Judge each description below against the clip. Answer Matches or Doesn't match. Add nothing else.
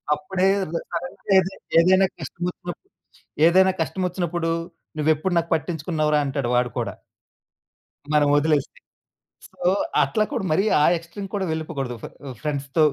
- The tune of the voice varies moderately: Matches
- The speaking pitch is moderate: Matches